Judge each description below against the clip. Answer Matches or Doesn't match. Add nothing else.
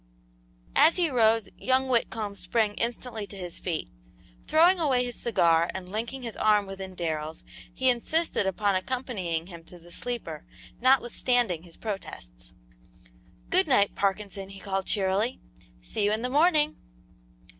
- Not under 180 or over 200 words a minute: Doesn't match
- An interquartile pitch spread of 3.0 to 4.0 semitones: Doesn't match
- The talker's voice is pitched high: Matches